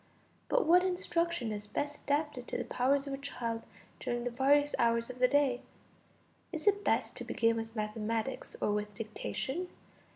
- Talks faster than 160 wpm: Yes, average, 170 wpm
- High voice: Yes, very high, 255 Hz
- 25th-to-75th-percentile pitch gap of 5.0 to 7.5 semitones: No, average, 4.3 semitones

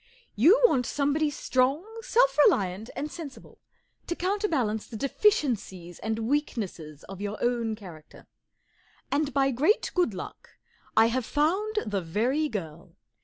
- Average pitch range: No, wide, 6.6 semitones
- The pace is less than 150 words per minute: Yes, average, 140 wpm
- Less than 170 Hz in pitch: No, very high, 250 Hz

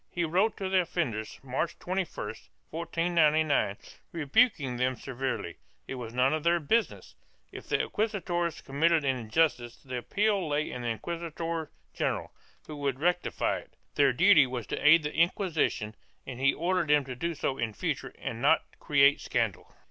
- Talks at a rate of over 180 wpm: No, average, 165 wpm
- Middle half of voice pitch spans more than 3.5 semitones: Yes, average, 4.7 semitones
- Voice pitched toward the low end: No, medium, 150 Hz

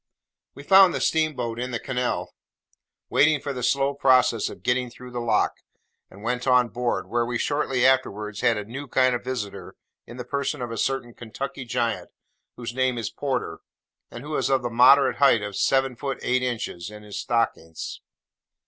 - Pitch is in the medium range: No, low, 125 Hz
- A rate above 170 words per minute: Yes, average, 185 wpm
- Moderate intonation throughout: No, narrow, 2.3 semitones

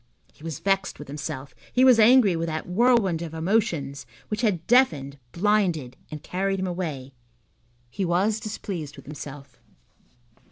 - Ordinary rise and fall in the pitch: No, wide, 6.0 semitones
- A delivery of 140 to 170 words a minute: Yes, average, 150 wpm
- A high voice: No, medium, 175 Hz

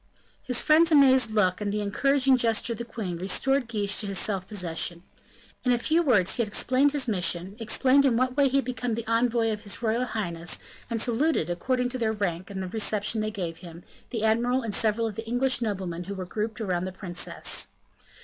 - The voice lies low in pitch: No, high, 220 Hz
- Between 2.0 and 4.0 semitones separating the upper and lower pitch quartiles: No, average, 4.6 semitones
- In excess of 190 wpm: Yes, fast, 205 wpm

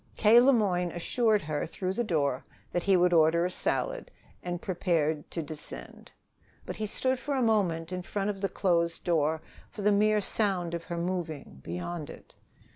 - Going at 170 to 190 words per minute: Yes, average, 185 wpm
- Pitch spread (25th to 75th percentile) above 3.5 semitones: Yes, average, 4.1 semitones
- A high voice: No, medium, 180 Hz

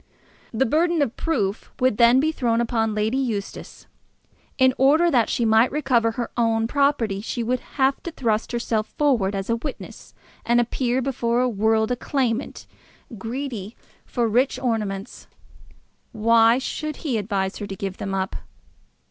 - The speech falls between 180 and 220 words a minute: No, average, 155 wpm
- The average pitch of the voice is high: Yes, high, 235 Hz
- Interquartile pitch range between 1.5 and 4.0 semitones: Yes, average, 3.2 semitones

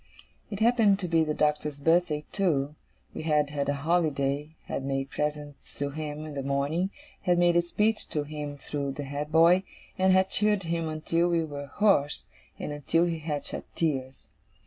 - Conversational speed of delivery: Yes, average, 185 wpm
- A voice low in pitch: No, medium, 155 Hz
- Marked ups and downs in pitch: No, average, 3.2 semitones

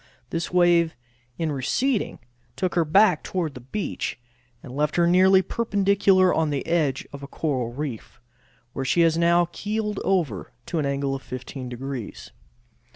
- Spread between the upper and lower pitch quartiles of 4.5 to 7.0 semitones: Yes, average, 5.2 semitones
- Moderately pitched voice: Yes, medium, 165 Hz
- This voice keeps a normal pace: Yes, average, 160 wpm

